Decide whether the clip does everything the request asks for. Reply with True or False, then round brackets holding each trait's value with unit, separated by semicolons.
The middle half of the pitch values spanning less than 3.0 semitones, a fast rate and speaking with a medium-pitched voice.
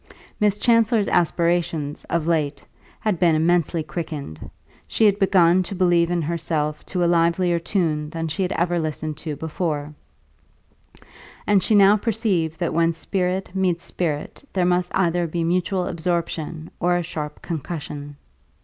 False (2.5 semitones; 150 wpm; 170 Hz)